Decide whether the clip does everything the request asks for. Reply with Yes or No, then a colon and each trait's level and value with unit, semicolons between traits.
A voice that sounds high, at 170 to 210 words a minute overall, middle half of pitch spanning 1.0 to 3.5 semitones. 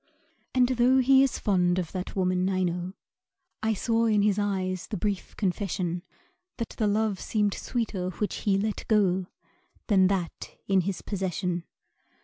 No: high, 195 Hz; average, 155 wpm; average, 2.9 semitones